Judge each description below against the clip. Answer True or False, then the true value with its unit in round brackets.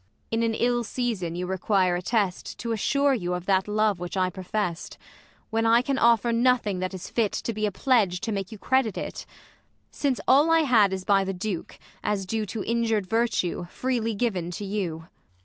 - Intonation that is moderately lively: True (3.9 semitones)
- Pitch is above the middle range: True (210 Hz)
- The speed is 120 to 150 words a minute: False (200 wpm)